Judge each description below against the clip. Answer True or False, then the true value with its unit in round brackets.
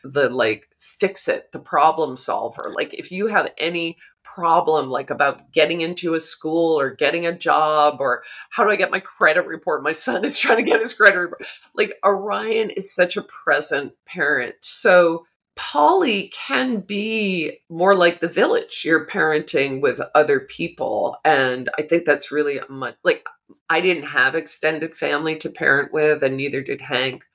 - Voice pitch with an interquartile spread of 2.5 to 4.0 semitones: False (4.7 semitones)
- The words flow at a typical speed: True (175 wpm)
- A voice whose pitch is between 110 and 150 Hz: False (165 Hz)